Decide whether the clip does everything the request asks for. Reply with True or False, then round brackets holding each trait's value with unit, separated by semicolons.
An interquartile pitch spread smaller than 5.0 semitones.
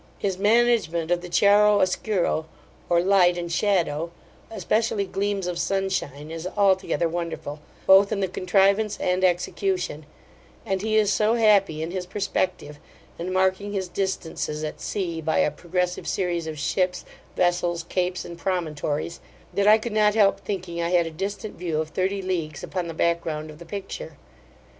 True (2.8 semitones)